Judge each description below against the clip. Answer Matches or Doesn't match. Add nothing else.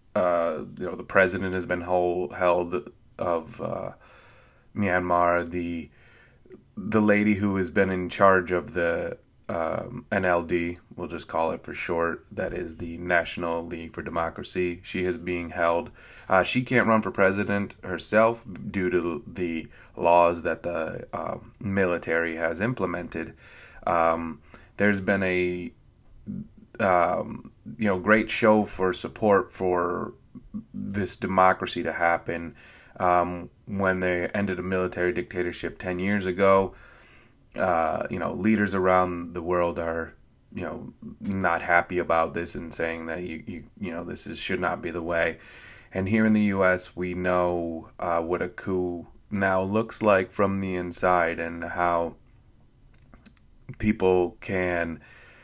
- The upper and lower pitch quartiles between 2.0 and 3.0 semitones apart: Matches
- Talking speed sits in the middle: Matches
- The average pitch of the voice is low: Matches